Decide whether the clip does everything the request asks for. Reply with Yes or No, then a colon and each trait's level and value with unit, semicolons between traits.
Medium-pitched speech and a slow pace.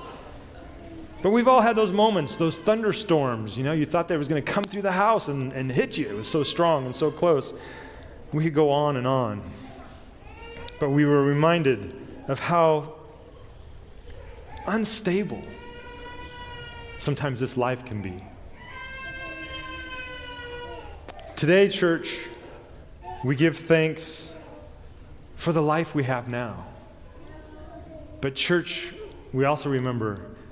Yes: medium, 150 Hz; slow, 130 wpm